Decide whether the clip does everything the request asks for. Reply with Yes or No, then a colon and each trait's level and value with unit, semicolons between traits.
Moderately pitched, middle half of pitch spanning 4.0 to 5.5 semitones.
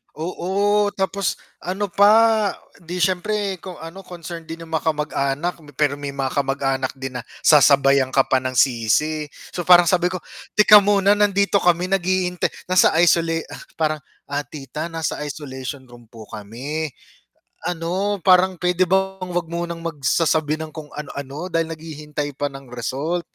Yes: medium, 165 Hz; average, 4.4 semitones